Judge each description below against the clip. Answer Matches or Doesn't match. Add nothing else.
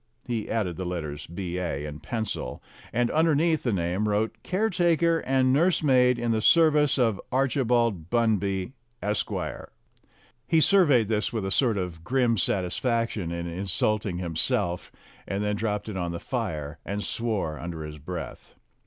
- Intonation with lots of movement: Matches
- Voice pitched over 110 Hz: Doesn't match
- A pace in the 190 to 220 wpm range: Doesn't match